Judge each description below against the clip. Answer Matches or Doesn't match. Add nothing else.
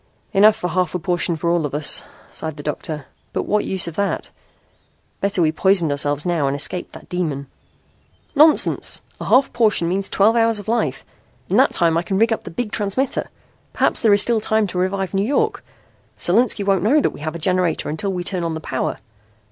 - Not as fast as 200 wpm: Doesn't match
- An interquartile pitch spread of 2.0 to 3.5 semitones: Doesn't match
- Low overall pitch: Doesn't match